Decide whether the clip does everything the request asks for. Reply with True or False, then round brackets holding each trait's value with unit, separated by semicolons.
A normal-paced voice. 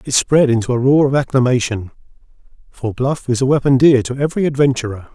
True (185 wpm)